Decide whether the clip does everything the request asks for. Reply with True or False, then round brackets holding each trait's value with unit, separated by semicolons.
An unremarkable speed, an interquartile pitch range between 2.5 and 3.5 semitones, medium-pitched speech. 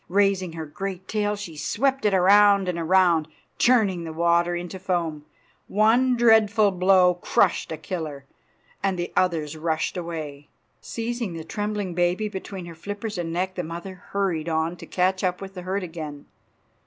True (165 wpm; 3.2 semitones; 180 Hz)